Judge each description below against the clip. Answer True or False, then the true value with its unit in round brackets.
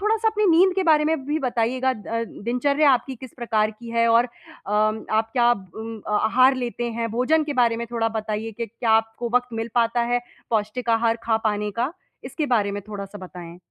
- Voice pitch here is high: True (235 Hz)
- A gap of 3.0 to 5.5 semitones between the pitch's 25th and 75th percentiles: False (2.6 semitones)